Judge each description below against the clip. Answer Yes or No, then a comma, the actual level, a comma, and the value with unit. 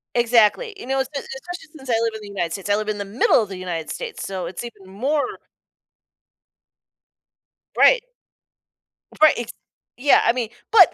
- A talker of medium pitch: No, high, 230 Hz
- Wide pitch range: Yes, wide, 5.7 semitones